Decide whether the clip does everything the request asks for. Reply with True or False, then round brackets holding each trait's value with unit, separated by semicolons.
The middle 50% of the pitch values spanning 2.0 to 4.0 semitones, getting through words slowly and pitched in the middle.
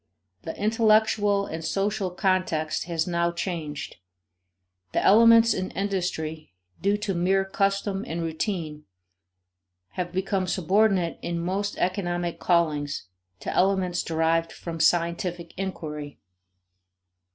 True (3.0 semitones; 105 wpm; 180 Hz)